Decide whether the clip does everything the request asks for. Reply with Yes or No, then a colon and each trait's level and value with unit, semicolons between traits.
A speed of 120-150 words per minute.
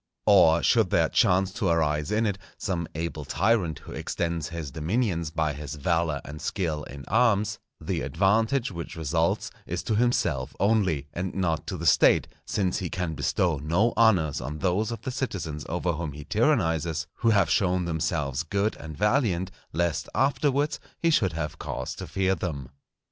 No: average, 170 wpm